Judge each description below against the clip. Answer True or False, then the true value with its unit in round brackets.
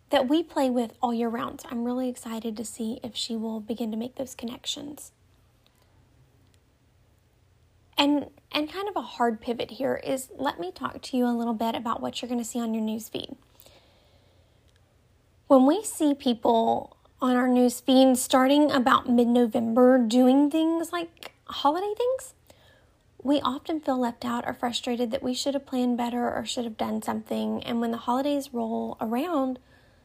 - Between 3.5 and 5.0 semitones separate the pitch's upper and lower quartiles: False (3.0 semitones)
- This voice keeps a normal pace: True (170 wpm)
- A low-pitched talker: False (245 Hz)